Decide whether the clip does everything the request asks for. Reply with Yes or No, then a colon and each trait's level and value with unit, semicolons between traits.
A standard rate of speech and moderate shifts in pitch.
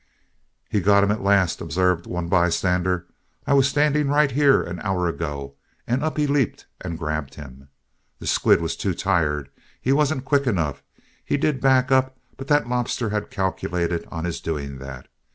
No: average, 175 wpm; wide, 8.2 semitones